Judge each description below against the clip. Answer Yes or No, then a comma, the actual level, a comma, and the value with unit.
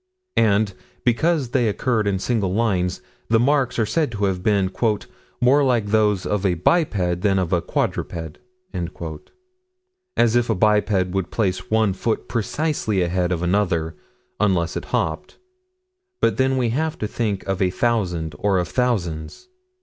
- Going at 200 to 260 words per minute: No, average, 155 wpm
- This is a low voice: Yes, low, 105 Hz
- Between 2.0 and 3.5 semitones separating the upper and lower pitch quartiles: No, average, 4.6 semitones